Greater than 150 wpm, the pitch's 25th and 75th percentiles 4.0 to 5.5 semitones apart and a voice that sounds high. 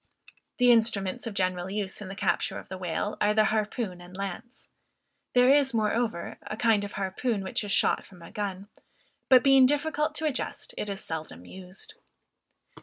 Yes: average, 180 wpm; average, 4.4 semitones; high, 210 Hz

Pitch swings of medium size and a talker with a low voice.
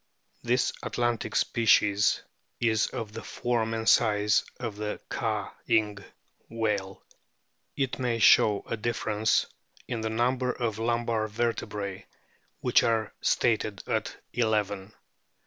No: narrow, 2.0 semitones; low, 110 Hz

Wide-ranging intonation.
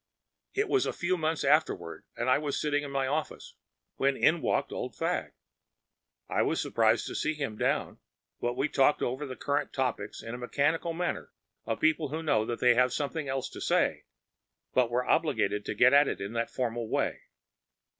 No: average, 4.0 semitones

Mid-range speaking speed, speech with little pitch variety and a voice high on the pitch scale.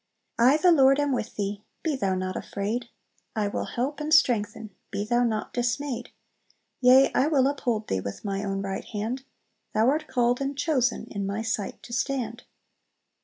No: average, 175 wpm; average, 4.6 semitones; high, 240 Hz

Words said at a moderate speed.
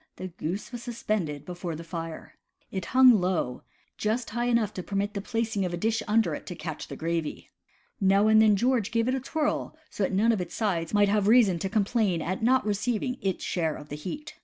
No: fast, 230 wpm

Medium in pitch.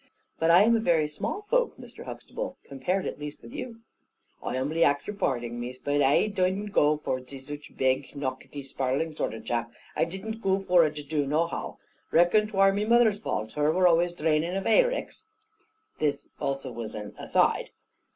Yes: medium, 155 Hz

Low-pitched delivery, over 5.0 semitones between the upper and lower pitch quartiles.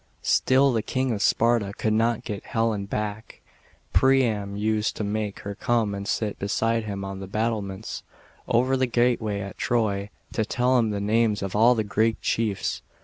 No: low, 110 Hz; narrow, 2.5 semitones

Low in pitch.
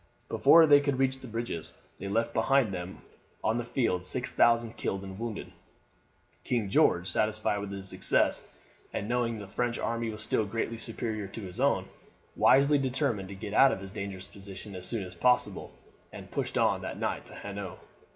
Yes: low, 110 Hz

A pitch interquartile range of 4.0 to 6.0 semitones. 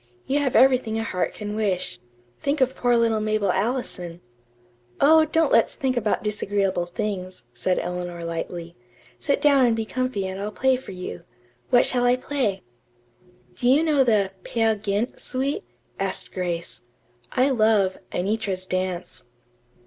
Yes: wide, 5.4 semitones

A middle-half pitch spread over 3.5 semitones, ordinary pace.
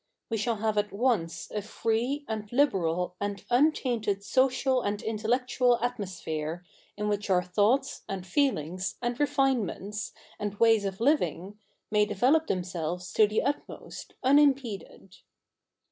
No: average, 4.5 semitones; slow, 130 wpm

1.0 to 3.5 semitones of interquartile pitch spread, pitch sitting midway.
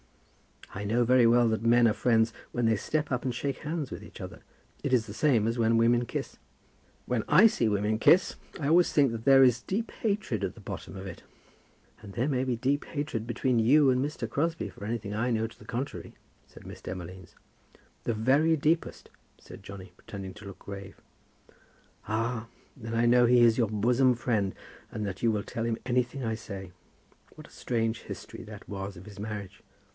No: average, 3.2 semitones; low, 115 Hz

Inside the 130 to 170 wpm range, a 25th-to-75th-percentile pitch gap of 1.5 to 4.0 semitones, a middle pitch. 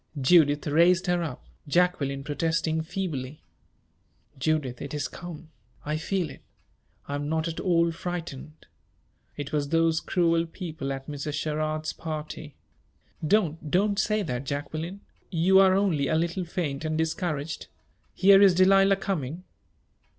Yes: average, 140 wpm; average, 3.2 semitones; medium, 160 Hz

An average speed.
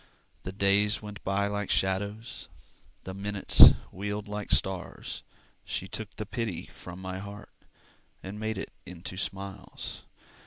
No: slow, 130 wpm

